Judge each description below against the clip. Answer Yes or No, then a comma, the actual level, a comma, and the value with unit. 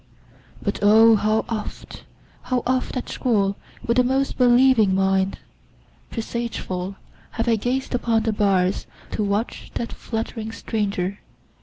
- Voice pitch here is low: No, high, 225 Hz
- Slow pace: Yes, slow, 125 wpm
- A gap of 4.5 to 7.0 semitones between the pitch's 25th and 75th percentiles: No, average, 3.2 semitones